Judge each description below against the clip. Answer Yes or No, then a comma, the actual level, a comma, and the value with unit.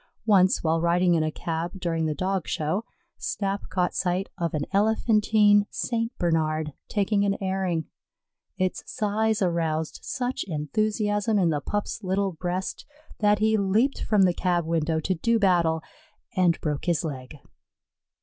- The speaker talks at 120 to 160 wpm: Yes, average, 150 wpm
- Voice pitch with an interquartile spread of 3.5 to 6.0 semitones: Yes, average, 4.1 semitones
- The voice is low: No, medium, 185 Hz